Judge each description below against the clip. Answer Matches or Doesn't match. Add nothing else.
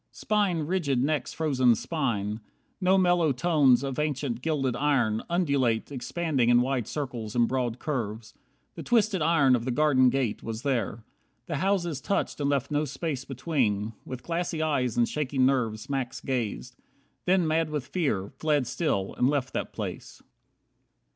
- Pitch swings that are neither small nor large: Matches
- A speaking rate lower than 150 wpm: Doesn't match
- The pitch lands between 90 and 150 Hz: Matches